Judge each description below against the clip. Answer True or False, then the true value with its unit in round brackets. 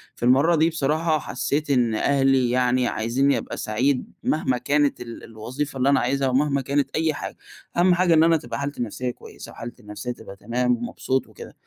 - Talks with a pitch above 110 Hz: True (135 Hz)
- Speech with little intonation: False (3.2 semitones)